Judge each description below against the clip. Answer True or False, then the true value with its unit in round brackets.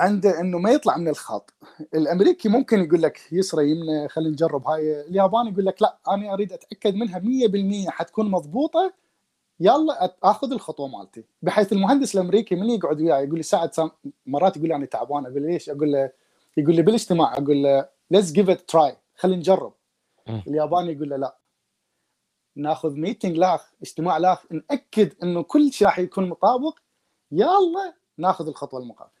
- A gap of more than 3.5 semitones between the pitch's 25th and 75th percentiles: True (5.5 semitones)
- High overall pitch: False (180 Hz)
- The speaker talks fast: True (160 wpm)